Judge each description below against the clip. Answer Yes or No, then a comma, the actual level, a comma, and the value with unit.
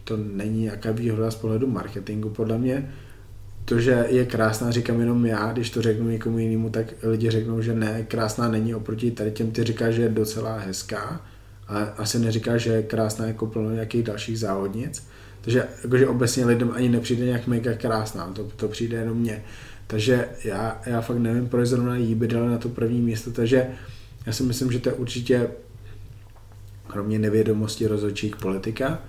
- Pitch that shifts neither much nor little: No, narrow, 1.7 semitones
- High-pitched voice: No, low, 115 Hz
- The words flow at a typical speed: No, fast, 185 wpm